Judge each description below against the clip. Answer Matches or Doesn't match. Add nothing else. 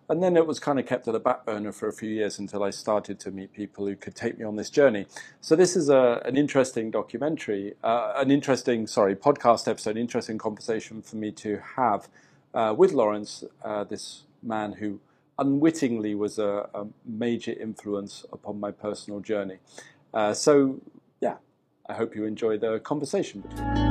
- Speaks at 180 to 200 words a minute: Matches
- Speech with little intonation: Doesn't match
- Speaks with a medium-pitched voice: Doesn't match